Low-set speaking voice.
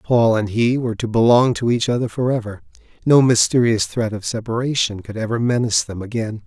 Yes: low, 115 Hz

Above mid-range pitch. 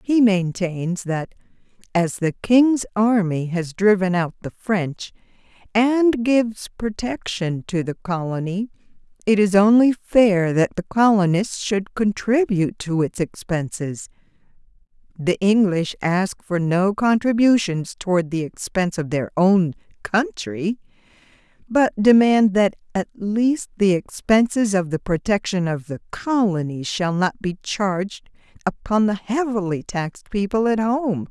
Yes: high, 195 Hz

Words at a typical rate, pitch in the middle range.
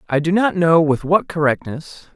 Yes: average, 195 wpm; medium, 165 Hz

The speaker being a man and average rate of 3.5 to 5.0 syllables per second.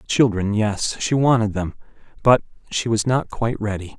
No: male; 5.3 syllables/s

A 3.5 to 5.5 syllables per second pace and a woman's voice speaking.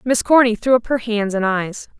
Yes: 5.0 syllables/s; female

